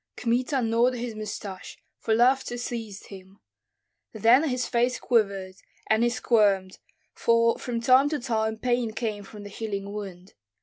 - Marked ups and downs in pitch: No, average, 3.0 semitones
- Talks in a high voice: Yes, high, 230 Hz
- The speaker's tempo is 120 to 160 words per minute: Yes, average, 145 wpm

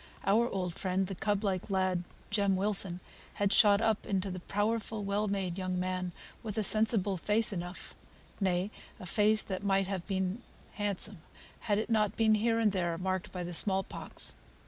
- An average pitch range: No, narrow, 2.2 semitones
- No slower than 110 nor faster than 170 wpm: No, average, 180 wpm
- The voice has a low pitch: No, high, 195 Hz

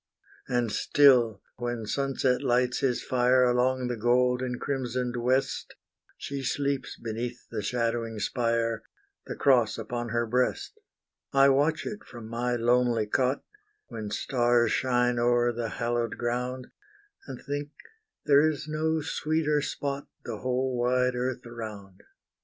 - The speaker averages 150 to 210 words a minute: No, slow, 135 wpm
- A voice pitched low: Yes, low, 125 Hz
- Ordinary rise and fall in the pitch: No, narrow, 2.0 semitones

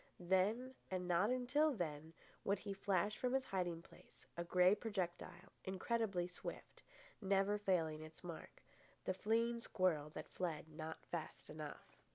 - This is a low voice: No, medium, 185 Hz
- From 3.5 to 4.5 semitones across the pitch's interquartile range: Yes, average, 3.8 semitones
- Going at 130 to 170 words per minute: Yes, average, 140 wpm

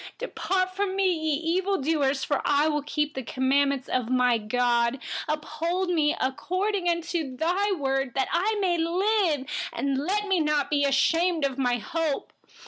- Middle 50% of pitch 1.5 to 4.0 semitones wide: No, average, 5.0 semitones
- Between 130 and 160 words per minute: Yes, average, 150 wpm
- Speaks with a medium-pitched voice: No, very high, 305 Hz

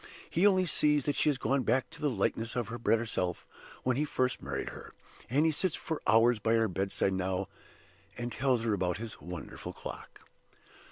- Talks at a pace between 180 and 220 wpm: Yes, average, 200 wpm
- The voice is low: Yes, low, 120 Hz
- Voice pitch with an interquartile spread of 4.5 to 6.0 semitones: Yes, wide, 5.4 semitones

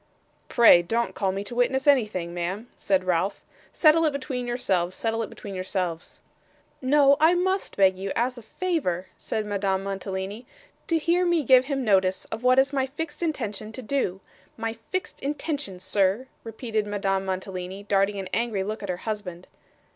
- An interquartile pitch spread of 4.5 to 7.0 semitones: Yes, wide, 5.6 semitones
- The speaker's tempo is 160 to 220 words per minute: Yes, average, 175 wpm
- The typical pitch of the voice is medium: No, high, 215 Hz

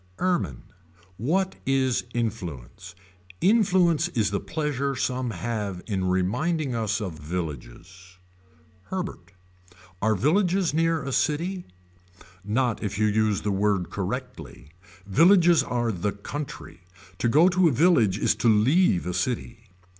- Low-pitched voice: Yes, low, 120 Hz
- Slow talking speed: Yes, slow, 125 wpm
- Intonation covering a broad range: Yes, wide, 8.2 semitones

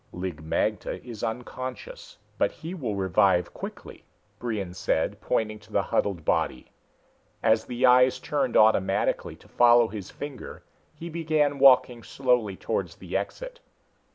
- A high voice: No, low, 120 Hz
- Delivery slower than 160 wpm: Yes, slow, 135 wpm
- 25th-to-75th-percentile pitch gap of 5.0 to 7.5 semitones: Yes, wide, 5.6 semitones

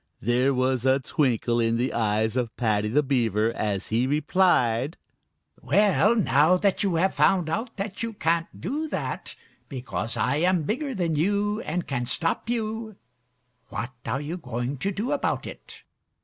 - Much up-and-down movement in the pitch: Yes, wide, 8.2 semitones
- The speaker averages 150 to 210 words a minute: Yes, average, 165 wpm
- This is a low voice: No, medium, 150 Hz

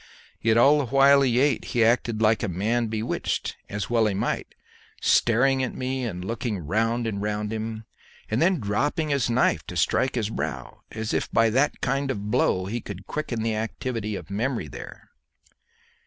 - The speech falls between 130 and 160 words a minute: No, average, 185 wpm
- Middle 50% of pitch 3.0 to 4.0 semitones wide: Yes, average, 3.5 semitones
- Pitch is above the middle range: No, low, 115 Hz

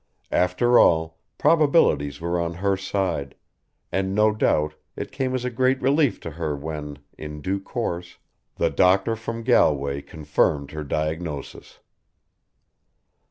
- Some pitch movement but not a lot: No, wide, 6.9 semitones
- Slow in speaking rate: Yes, slow, 130 wpm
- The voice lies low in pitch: Yes, very low, 90 Hz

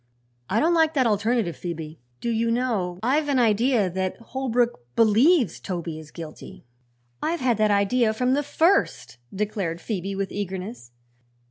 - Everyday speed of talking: Yes, average, 150 wpm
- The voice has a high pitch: Yes, high, 220 Hz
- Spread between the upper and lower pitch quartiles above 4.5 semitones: Yes, average, 5.1 semitones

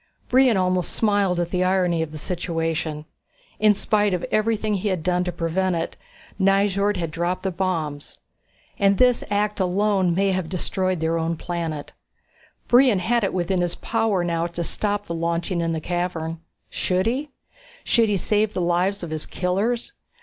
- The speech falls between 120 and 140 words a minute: No, average, 170 wpm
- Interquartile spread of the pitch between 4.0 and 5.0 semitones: No, average, 3.3 semitones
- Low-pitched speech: No, medium, 185 Hz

